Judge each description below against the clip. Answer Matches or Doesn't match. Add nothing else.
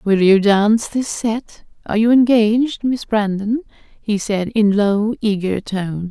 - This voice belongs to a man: Doesn't match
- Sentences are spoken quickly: Doesn't match